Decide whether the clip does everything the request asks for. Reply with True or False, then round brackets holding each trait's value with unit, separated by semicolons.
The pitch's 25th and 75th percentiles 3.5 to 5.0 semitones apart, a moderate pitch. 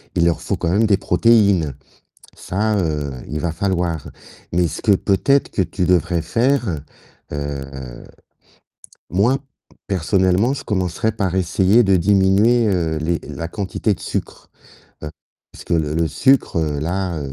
False (3.8 semitones; 95 Hz)